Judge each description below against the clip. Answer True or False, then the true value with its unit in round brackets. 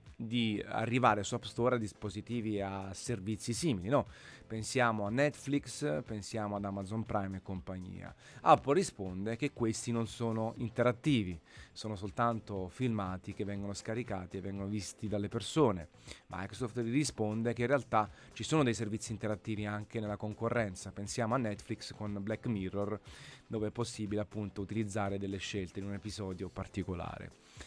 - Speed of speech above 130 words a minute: True (150 wpm)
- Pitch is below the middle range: True (105 Hz)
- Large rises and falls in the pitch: False (2.9 semitones)